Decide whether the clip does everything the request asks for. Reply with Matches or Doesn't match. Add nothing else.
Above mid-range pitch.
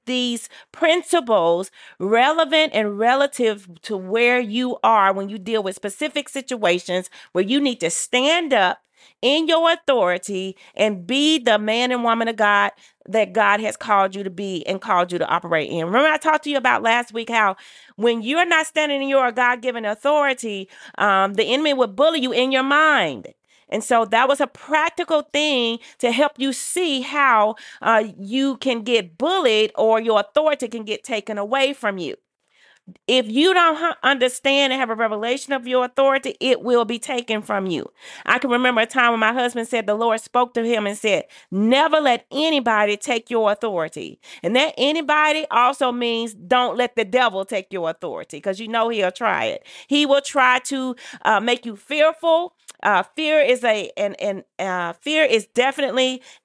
Matches